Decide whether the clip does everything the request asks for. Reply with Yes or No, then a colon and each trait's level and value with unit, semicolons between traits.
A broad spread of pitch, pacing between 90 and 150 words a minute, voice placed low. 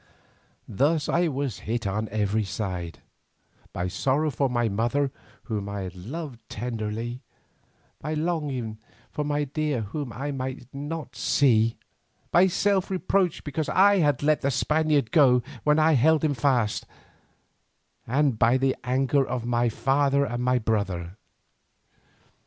No: average, 4.8 semitones; average, 140 wpm; low, 130 Hz